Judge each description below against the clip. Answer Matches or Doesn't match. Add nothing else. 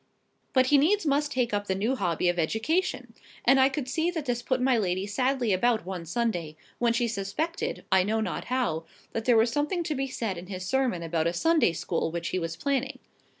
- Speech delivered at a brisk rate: Matches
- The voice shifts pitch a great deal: Matches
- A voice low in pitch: Doesn't match